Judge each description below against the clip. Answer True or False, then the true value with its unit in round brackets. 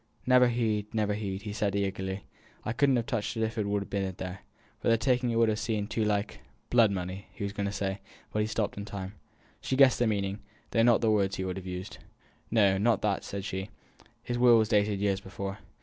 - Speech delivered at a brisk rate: True (235 wpm)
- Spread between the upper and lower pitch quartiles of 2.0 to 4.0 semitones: True (2.6 semitones)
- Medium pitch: False (105 Hz)